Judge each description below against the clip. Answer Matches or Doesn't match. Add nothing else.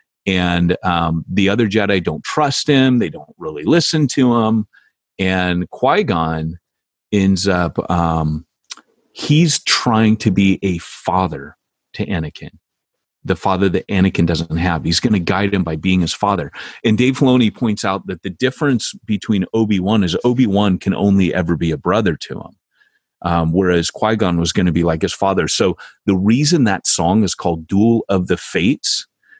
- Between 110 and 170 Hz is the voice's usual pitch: Doesn't match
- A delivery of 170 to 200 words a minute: Matches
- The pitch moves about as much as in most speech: Matches